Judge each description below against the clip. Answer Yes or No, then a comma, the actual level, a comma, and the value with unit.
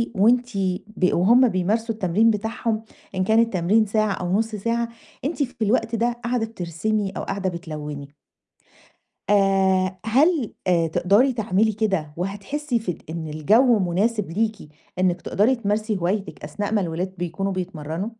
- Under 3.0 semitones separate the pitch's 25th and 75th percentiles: No, average, 3.7 semitones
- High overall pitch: Yes, high, 205 Hz